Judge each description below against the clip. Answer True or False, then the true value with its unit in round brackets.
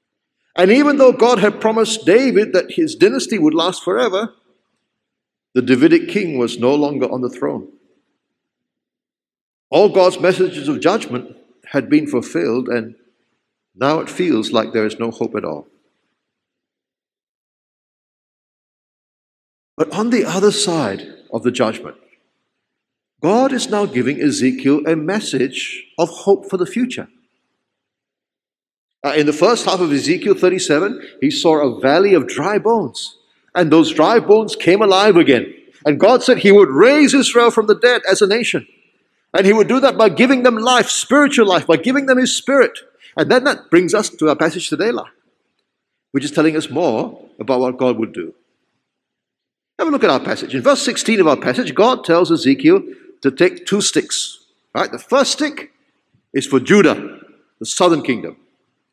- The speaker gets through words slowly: False (165 wpm)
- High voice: True (205 Hz)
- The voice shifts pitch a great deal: True (8.0 semitones)